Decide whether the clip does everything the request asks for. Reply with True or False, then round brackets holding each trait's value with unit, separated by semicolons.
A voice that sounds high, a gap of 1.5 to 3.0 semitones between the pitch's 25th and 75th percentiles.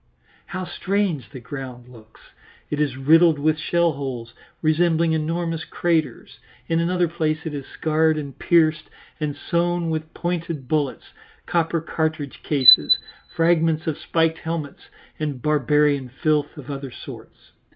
False (155 Hz; 2.7 semitones)